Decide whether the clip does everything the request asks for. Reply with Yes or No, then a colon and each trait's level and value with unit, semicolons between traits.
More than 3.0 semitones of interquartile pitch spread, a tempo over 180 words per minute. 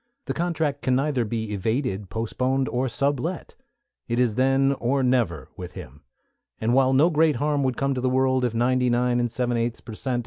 No: narrow, 2.6 semitones; average, 200 wpm